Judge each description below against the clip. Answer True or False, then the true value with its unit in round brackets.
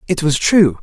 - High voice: False (160 Hz)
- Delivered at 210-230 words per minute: True (220 wpm)